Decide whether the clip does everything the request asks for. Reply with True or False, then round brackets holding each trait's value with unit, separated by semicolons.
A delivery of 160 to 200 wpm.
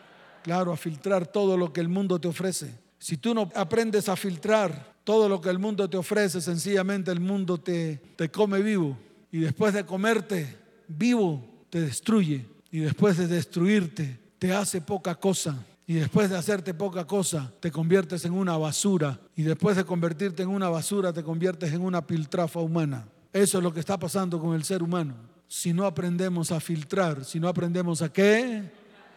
True (185 wpm)